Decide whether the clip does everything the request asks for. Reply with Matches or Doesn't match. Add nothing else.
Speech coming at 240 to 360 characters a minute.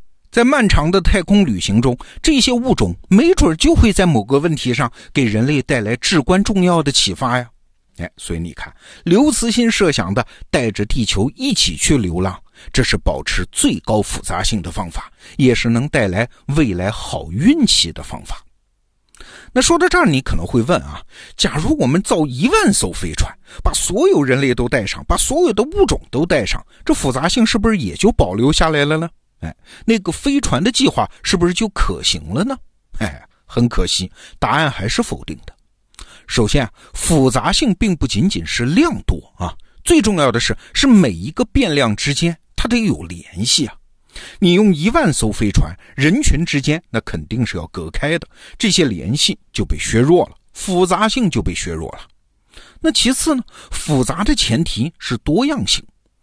Matches